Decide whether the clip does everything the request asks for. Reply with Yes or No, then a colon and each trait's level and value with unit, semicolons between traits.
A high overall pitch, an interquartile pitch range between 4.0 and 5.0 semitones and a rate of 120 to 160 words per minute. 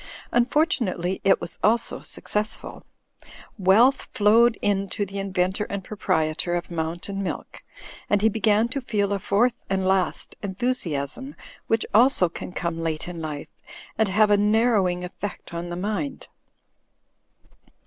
No: high, 200 Hz; average, 3.6 semitones; average, 140 wpm